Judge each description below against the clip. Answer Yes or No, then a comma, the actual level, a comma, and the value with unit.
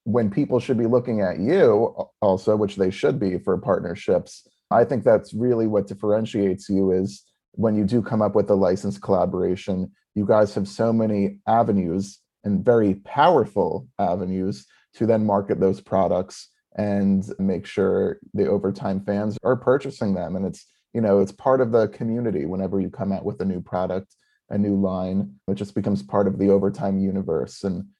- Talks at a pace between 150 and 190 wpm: Yes, average, 180 wpm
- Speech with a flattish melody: Yes, narrow, 2.3 semitones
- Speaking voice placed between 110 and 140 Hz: No, low, 100 Hz